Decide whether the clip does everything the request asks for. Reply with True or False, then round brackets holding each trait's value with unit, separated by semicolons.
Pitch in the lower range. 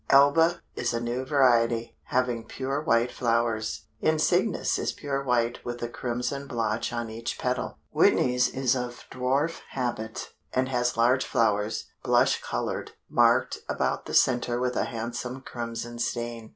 True (120 Hz)